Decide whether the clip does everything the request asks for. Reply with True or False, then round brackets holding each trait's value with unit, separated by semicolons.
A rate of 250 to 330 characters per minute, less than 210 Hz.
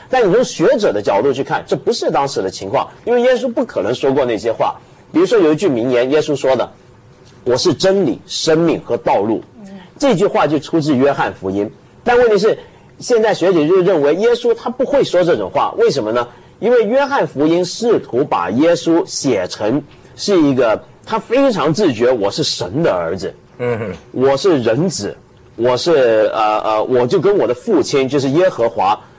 True (275 characters per minute; 185 Hz)